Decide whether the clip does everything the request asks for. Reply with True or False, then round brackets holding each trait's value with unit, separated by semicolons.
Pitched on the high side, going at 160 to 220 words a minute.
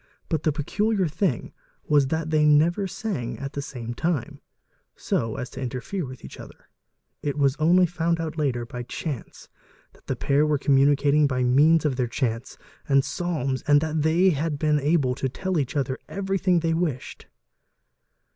False (150 Hz; 170 wpm)